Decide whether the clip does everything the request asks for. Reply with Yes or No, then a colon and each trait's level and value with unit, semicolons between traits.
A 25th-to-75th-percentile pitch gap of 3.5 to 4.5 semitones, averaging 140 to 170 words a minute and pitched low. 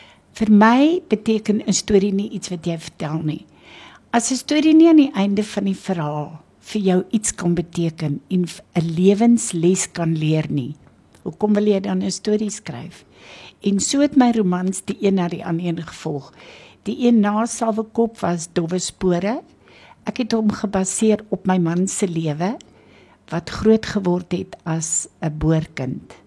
No: average, 4.1 semitones; average, 165 wpm; high, 195 Hz